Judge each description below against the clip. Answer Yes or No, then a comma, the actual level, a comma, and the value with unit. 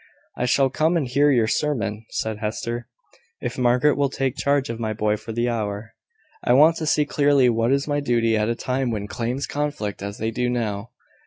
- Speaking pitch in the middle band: No, low, 120 Hz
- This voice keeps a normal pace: No, fast, 210 wpm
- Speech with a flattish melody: No, average, 4.1 semitones